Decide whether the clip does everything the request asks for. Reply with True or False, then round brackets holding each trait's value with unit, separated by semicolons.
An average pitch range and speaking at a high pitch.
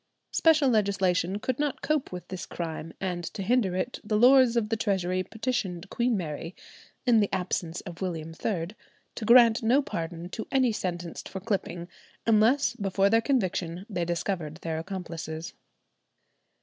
True (4.8 semitones; 195 Hz)